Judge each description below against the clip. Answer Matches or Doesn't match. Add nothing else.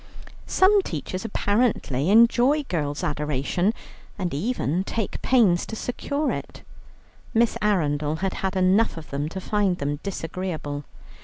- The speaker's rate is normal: Doesn't match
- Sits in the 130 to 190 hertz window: Matches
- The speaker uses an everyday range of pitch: Doesn't match